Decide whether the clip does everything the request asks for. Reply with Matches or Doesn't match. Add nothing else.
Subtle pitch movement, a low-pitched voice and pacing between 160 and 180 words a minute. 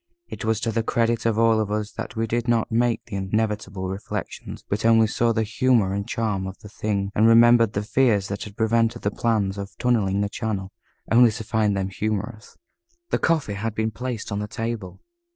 Doesn't match